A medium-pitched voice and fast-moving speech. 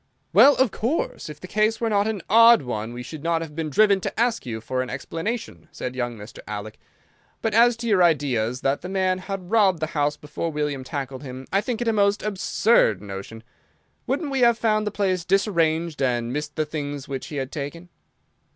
Yes: medium, 165 Hz; fast, 210 wpm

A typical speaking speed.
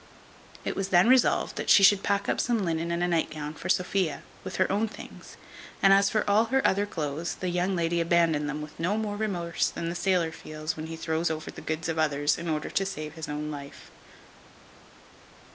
No: fast, 215 wpm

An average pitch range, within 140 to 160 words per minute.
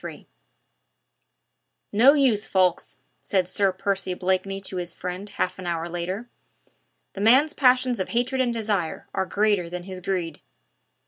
Yes: average, 3.8 semitones; average, 145 wpm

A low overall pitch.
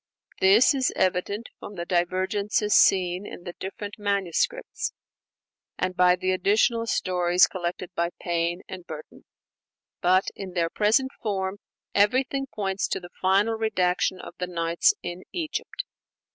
No: high, 190 Hz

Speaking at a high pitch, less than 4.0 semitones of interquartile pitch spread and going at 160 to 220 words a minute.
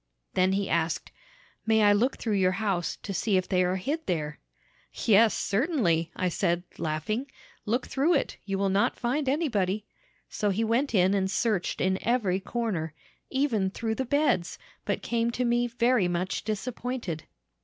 No: high, 205 Hz; average, 4.5 semitones; average, 165 wpm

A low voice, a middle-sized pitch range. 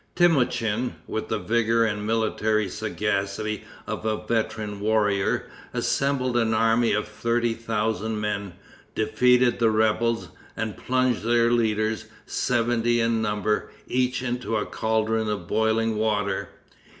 No: low, 110 Hz; narrow, 1.8 semitones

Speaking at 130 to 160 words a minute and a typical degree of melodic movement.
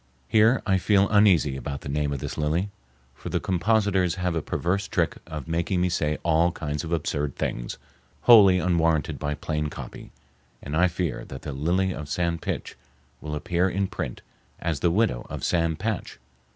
No: average, 180 wpm; average, 3.9 semitones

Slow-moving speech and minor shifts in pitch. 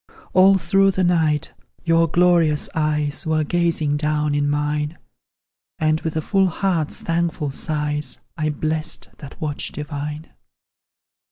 Yes: slow, 125 wpm; narrow, 2.3 semitones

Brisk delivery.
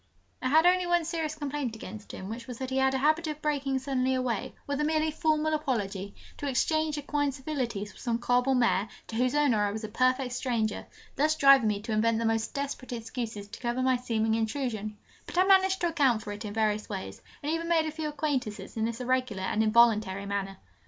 Yes: fast, 220 wpm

